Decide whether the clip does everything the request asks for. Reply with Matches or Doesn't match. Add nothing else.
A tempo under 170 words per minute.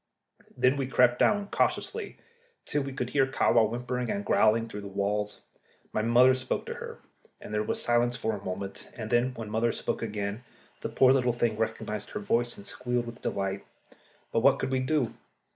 Doesn't match